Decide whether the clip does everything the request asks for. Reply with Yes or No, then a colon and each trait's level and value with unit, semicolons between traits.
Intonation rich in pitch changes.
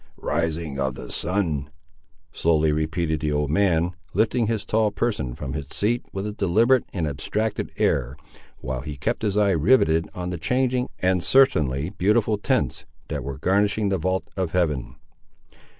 Yes: wide, 5.7 semitones